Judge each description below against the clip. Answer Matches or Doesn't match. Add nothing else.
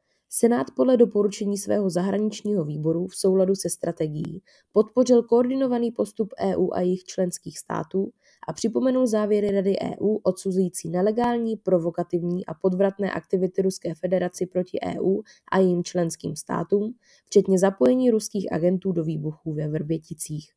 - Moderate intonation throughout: Matches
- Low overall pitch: Doesn't match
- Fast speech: Doesn't match